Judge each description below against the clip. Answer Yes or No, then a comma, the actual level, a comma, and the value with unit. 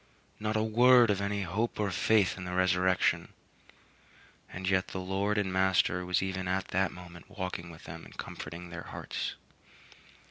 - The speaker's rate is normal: Yes, average, 170 wpm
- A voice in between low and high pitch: No, very low, 95 Hz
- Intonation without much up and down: Yes, narrow, 2.0 semitones